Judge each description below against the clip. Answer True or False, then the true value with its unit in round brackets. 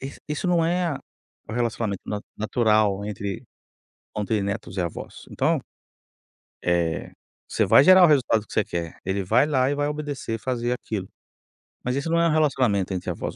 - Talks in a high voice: False (115 Hz)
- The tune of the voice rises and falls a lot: True (6.4 semitones)